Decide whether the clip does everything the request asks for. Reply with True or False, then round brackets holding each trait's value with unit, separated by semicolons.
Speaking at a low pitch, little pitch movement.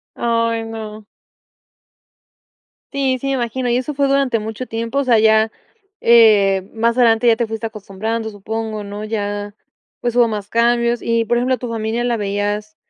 False (225 Hz; 2.0 semitones)